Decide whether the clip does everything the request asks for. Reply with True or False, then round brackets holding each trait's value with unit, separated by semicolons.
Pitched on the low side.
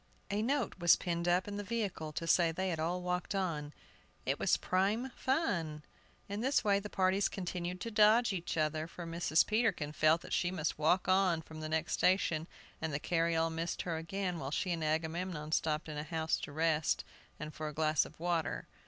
False (170 Hz)